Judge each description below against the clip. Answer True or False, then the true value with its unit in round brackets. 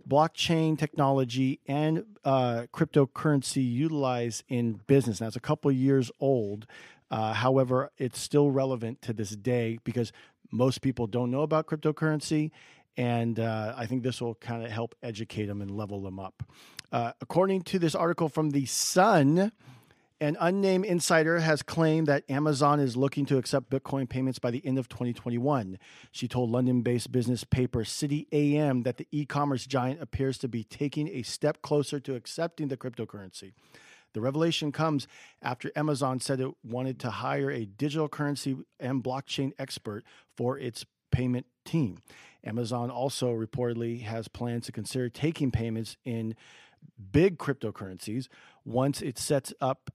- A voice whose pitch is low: True (130 Hz)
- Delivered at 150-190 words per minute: True (155 wpm)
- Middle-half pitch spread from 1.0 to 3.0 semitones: False (3.6 semitones)